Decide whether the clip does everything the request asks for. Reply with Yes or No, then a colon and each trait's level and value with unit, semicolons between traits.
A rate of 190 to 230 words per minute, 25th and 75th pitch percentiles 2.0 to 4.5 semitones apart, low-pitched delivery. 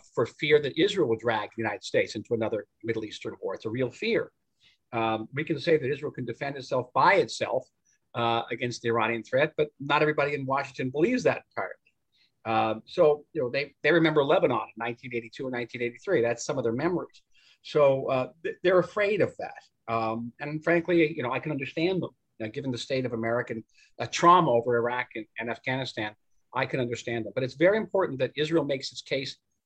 No: average, 200 wpm; average, 5.0 semitones; low, 130 Hz